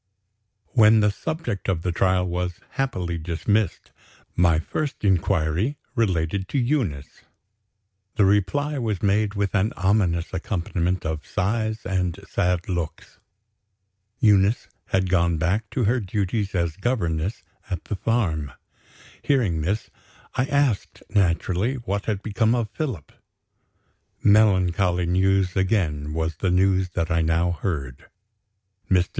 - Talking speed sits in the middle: No, slow, 125 wpm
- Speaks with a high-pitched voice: No, very low, 95 Hz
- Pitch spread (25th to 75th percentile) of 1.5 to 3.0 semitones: No, average, 3.9 semitones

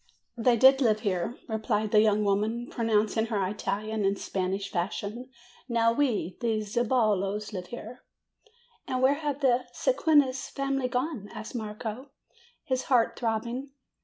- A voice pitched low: No, high, 225 Hz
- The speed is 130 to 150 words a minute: Yes, average, 140 wpm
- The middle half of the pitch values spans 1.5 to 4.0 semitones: Yes, average, 3.4 semitones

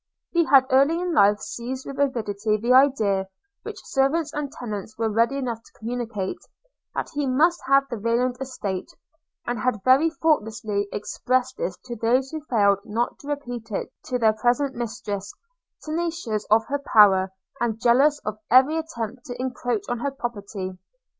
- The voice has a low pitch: No, high, 245 Hz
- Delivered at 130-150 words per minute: No, average, 165 wpm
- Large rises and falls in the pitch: No, average, 4.3 semitones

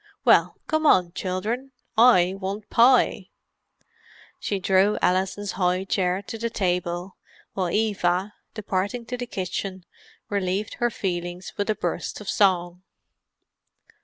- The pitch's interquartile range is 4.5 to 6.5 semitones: No, average, 2.9 semitones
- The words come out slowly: Yes, slow, 120 wpm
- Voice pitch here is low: No, high, 195 Hz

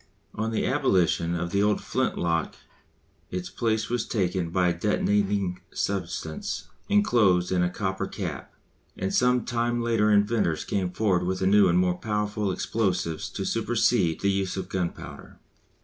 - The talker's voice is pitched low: Yes, very low, 95 Hz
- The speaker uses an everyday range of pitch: Yes, average, 3.1 semitones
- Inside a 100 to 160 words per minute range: Yes, average, 150 wpm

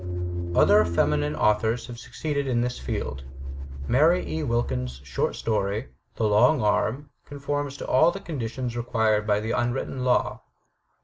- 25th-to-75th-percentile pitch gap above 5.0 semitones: No, average, 4.3 semitones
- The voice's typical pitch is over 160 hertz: No, low, 120 Hz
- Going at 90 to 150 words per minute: Yes, average, 140 wpm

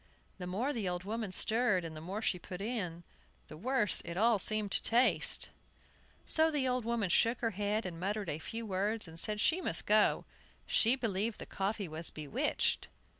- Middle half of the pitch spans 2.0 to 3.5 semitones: No, average, 4.2 semitones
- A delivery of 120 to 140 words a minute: No, average, 190 wpm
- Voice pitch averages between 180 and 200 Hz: No, high, 210 Hz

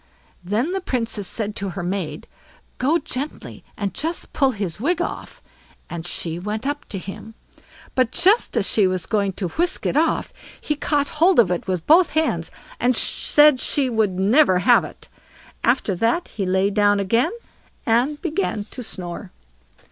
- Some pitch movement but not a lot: No, wide, 7.3 semitones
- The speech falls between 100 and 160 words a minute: No, average, 170 wpm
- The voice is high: Yes, high, 225 Hz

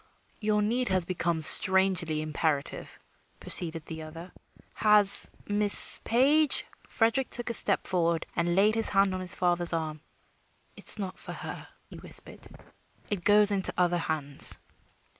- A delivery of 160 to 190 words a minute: No, average, 150 wpm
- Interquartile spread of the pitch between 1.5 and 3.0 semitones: No, average, 4.0 semitones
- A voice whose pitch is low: No, medium, 185 Hz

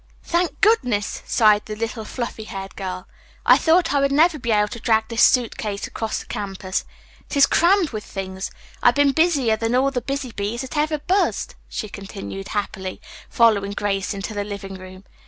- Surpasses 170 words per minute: Yes, average, 190 wpm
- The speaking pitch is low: No, high, 220 Hz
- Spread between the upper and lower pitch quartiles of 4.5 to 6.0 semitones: Yes, wide, 5.5 semitones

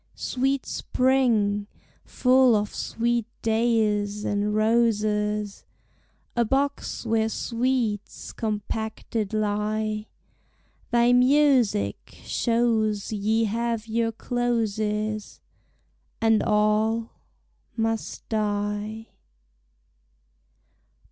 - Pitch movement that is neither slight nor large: No, narrow, 2.0 semitones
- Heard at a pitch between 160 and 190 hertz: No, high, 220 Hz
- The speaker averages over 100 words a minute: No, slow, 70 wpm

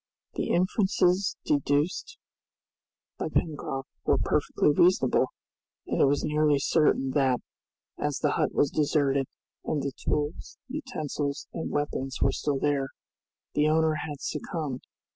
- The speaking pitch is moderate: Yes, medium, 150 Hz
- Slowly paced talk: Yes, slow, 125 wpm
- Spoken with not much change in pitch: Yes, narrow, 2.3 semitones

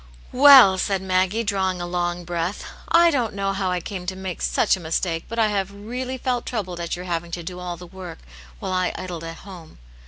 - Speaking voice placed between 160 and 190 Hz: Yes, medium, 185 Hz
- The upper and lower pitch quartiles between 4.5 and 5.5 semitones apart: No, average, 2.7 semitones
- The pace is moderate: No, fast, 230 wpm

